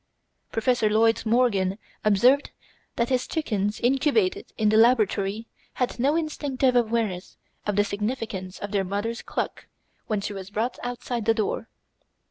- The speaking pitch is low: No, high, 225 Hz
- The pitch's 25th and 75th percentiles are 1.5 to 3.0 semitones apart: No, average, 3.4 semitones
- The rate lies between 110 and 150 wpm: Yes, average, 140 wpm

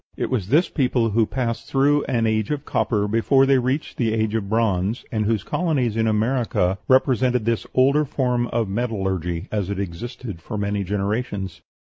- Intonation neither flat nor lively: Yes, average, 3.9 semitones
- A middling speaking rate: Yes, average, 175 wpm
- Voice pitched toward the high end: No, low, 115 Hz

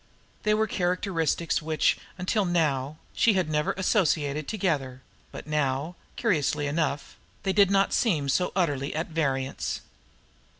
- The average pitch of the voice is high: No, medium, 160 Hz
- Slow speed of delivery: Yes, slow, 130 wpm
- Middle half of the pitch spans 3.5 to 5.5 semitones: Yes, average, 4.7 semitones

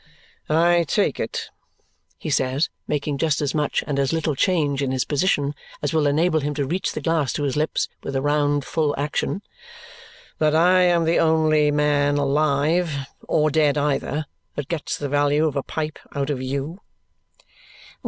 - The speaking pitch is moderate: Yes, medium, 150 Hz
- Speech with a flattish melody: Yes, narrow, 2.0 semitones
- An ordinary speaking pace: Yes, average, 175 wpm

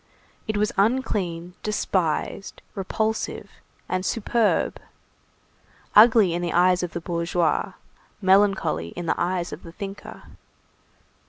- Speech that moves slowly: Yes, slow, 110 wpm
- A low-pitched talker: No, medium, 185 Hz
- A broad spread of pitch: No, average, 3.4 semitones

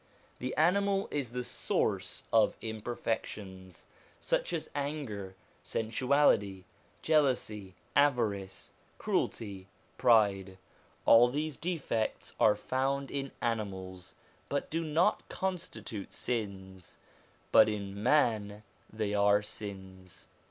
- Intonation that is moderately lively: No, wide, 6.0 semitones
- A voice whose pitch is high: No, low, 110 Hz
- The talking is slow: Yes, slow, 95 wpm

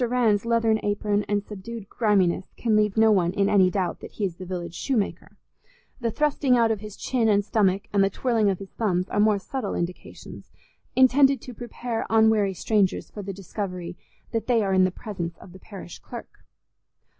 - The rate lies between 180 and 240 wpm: Yes, average, 190 wpm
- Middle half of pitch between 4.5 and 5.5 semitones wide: No, average, 3.0 semitones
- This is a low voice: No, high, 205 Hz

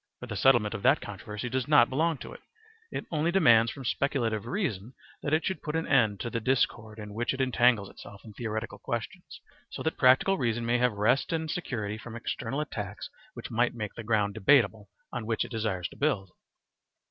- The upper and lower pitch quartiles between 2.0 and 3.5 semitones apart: No, average, 4.0 semitones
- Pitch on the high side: No, low, 120 Hz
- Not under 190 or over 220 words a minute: Yes, fast, 205 wpm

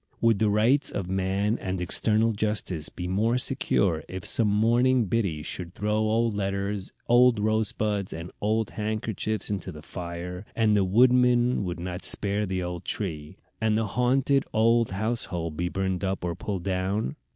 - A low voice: Yes, low, 105 Hz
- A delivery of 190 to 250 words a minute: No, average, 165 wpm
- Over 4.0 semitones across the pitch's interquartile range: No, average, 3.4 semitones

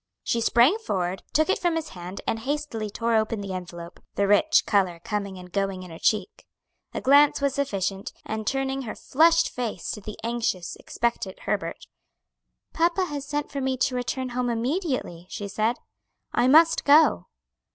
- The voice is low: No, high, 235 Hz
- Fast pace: No, average, 170 wpm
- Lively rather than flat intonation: Yes, wide, 6.2 semitones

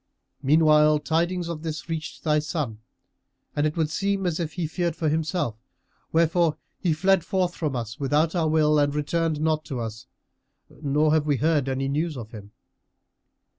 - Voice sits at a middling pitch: Yes, medium, 155 Hz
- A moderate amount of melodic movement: No, narrow, 2.2 semitones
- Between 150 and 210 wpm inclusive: Yes, average, 170 wpm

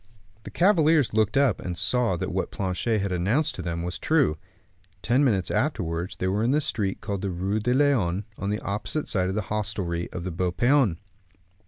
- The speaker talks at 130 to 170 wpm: No, average, 200 wpm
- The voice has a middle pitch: No, low, 105 Hz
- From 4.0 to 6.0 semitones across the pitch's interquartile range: Yes, wide, 5.4 semitones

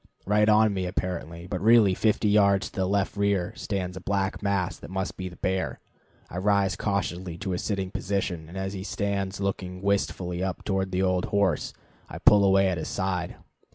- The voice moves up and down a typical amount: No, narrow, 1.6 semitones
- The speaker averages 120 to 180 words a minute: No, average, 195 wpm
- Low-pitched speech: Yes, very low, 95 Hz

